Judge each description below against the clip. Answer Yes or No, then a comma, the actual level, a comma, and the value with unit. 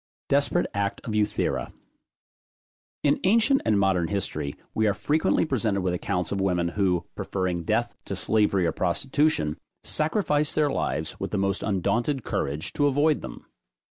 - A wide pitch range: Yes, wide, 7.7 semitones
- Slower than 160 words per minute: Yes, average, 150 wpm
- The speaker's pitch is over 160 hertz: No, low, 105 Hz